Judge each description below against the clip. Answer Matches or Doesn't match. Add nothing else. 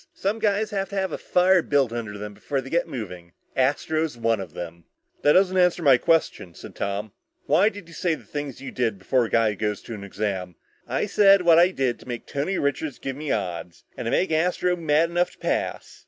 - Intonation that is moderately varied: Doesn't match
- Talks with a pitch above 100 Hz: Matches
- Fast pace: Matches